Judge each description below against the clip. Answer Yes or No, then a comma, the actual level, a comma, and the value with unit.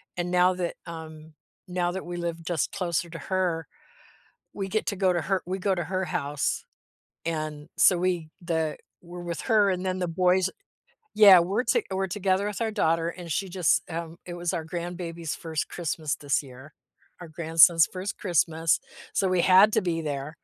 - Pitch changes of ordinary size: No, narrow, 2.3 semitones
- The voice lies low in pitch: No, medium, 175 Hz